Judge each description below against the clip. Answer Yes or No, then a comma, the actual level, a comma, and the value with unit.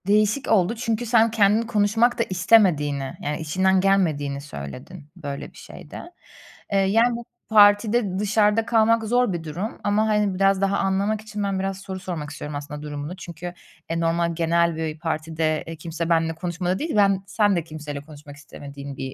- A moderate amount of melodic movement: Yes, average, 5.0 semitones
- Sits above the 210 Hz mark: No, medium, 185 Hz